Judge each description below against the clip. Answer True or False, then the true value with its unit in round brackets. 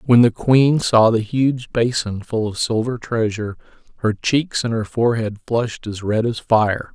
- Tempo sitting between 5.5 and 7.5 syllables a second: False (4.5 syllables/s)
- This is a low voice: True (115 Hz)